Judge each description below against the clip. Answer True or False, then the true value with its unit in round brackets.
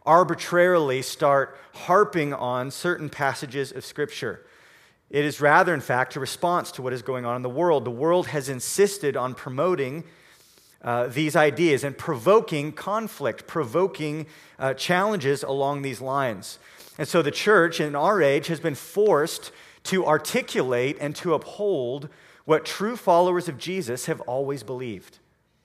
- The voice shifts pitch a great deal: False (4.5 semitones)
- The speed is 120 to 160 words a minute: True (150 wpm)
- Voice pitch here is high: False (150 Hz)